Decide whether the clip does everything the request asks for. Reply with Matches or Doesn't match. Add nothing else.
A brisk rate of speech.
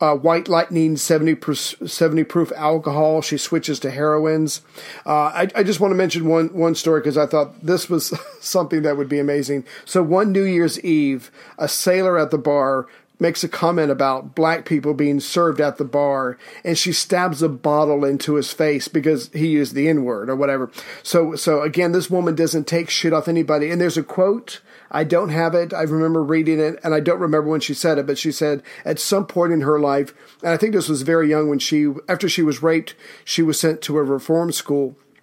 Matches